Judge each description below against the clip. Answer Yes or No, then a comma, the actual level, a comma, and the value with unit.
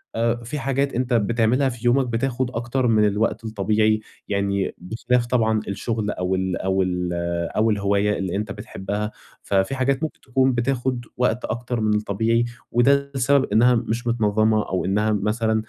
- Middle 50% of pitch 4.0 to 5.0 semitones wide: No, average, 3.0 semitones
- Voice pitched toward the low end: Yes, low, 115 Hz